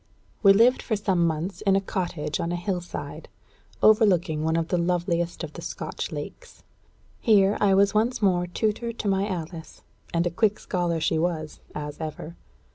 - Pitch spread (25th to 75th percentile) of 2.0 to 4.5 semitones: Yes, average, 3.2 semitones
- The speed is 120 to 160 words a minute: No, average, 180 wpm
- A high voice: No, medium, 180 Hz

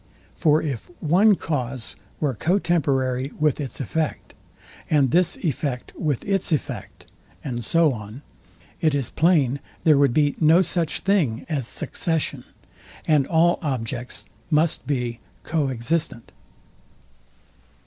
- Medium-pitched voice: Yes, medium, 145 Hz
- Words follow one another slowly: Yes, slow, 125 wpm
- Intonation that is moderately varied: Yes, average, 4.0 semitones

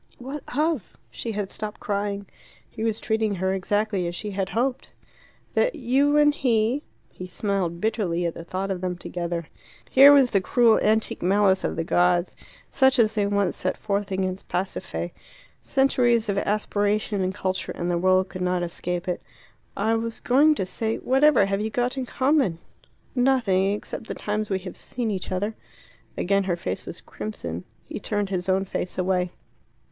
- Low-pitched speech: No, high, 200 Hz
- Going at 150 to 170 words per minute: No, average, 180 wpm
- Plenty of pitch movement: No, average, 3.8 semitones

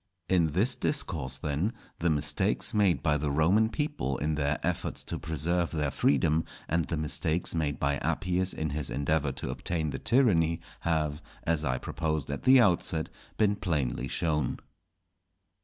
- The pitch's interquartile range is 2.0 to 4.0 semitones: Yes, average, 3.2 semitones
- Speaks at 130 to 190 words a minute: Yes, average, 155 wpm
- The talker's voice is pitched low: Yes, very low, 80 Hz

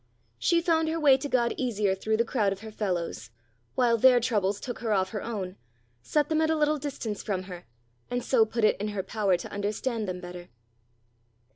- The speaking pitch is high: Yes, high, 220 Hz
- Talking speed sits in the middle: No, fast, 210 wpm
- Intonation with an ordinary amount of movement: Yes, average, 4.9 semitones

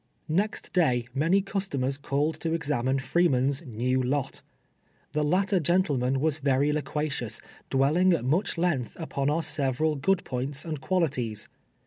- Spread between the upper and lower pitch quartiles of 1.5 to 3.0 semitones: No, average, 4.0 semitones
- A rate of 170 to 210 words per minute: No, average, 145 wpm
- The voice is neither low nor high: Yes, medium, 145 Hz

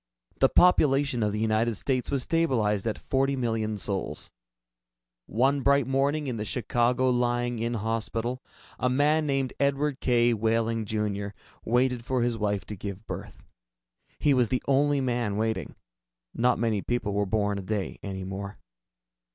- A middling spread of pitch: Yes, average, 3.8 semitones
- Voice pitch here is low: Yes, low, 120 Hz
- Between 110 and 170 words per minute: Yes, average, 155 wpm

